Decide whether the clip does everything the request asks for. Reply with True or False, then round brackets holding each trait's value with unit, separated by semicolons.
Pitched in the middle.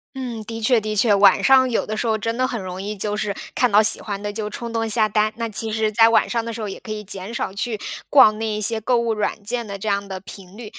False (215 Hz)